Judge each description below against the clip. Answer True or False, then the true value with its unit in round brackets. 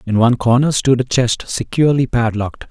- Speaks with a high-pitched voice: False (125 Hz)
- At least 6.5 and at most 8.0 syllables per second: False (5.9 syllables/s)